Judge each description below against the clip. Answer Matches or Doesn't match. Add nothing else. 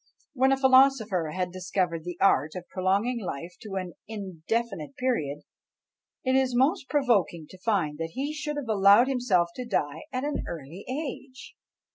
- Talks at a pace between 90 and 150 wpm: Doesn't match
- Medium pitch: Doesn't match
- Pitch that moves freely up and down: Matches